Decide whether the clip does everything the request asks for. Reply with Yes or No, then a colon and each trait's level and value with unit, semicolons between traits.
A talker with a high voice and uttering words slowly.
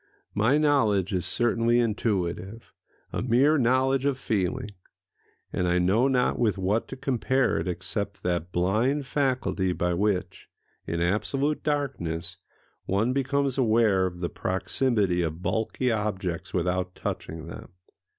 No: low, 105 Hz; slow, 130 wpm